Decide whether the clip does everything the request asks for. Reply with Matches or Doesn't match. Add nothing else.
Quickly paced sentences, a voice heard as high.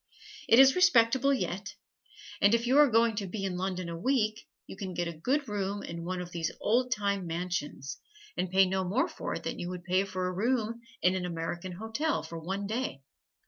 Matches